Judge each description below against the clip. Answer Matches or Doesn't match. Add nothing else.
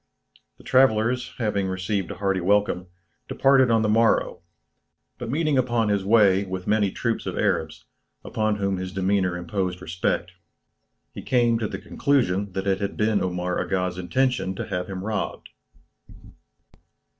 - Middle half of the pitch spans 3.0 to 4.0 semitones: Matches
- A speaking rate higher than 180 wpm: Doesn't match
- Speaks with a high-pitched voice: Doesn't match